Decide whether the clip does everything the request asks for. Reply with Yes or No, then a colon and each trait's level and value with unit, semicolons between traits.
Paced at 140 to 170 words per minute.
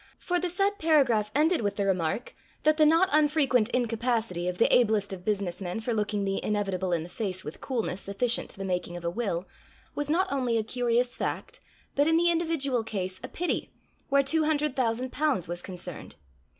No: average, 200 wpm